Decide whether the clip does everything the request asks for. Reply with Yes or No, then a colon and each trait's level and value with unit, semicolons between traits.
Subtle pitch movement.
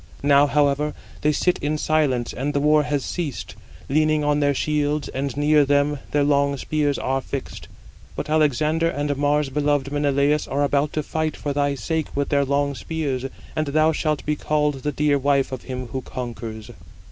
Yes: narrow, 1.4 semitones